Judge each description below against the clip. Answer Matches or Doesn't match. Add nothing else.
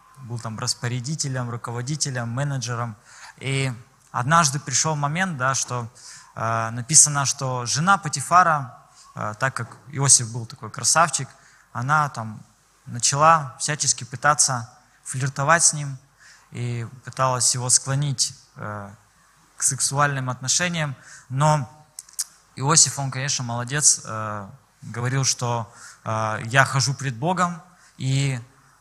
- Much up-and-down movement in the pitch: Doesn't match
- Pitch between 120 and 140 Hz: Matches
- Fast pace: Doesn't match